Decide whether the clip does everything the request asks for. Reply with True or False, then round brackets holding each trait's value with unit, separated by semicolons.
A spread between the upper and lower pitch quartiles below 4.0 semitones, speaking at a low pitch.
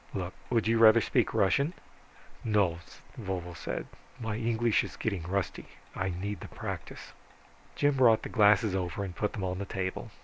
True (3.4 semitones; 100 Hz)